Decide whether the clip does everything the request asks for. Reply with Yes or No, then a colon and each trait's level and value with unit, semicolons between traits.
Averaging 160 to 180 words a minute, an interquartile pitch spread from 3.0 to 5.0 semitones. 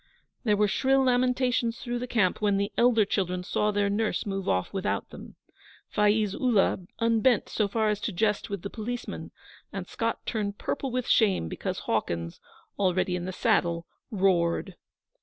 Yes: average, 165 wpm; average, 3.3 semitones